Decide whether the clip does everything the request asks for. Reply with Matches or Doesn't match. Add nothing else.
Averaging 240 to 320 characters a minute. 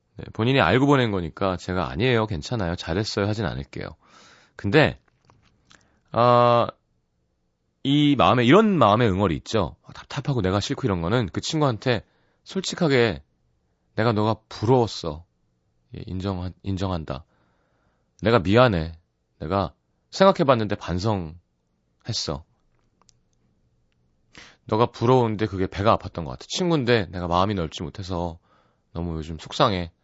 Matches